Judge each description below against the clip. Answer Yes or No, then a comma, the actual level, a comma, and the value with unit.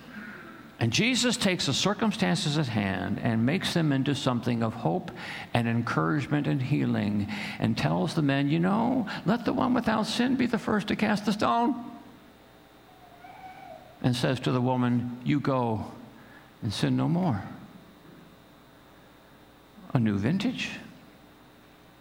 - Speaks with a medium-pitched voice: Yes, medium, 145 Hz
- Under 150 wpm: Yes, slow, 135 wpm